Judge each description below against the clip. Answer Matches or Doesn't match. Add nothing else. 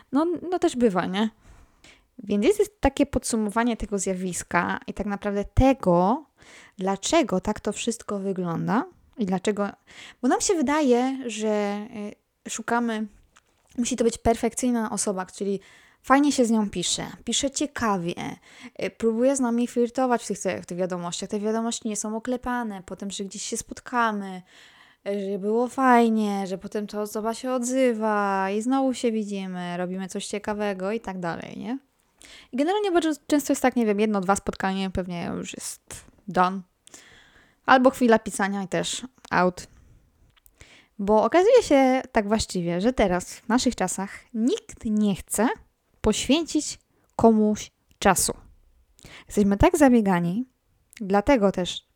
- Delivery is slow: Doesn't match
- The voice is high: Matches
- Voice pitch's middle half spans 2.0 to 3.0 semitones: Doesn't match